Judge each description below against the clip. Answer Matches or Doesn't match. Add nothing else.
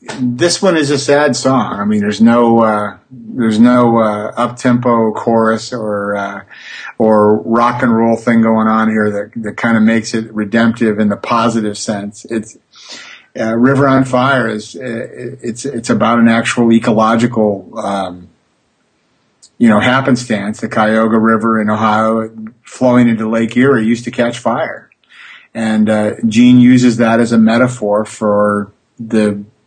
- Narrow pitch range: Matches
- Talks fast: Doesn't match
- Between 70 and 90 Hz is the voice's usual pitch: Doesn't match